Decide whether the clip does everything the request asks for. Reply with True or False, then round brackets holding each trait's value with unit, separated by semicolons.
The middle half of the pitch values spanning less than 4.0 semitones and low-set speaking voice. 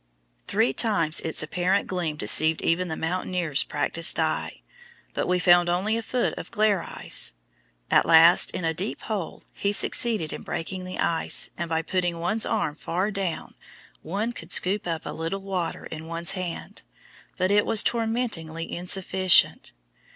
False (3.3 semitones; 180 Hz)